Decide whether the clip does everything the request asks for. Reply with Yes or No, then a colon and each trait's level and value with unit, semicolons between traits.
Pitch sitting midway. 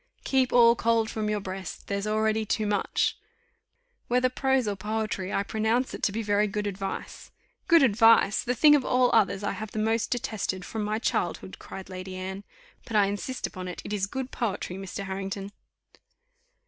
No: high, 210 Hz